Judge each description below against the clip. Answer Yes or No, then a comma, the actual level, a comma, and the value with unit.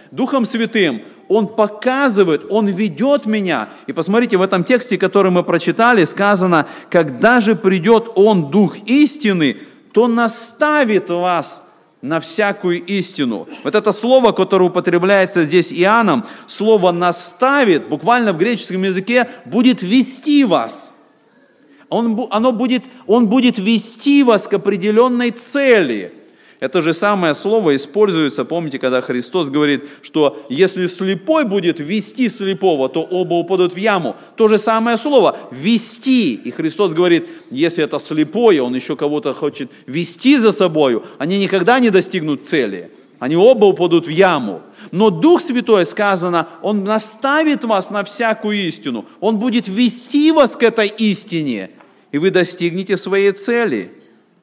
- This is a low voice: No, high, 205 Hz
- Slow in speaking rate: No, average, 135 wpm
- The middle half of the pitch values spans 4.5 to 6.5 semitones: Yes, average, 4.8 semitones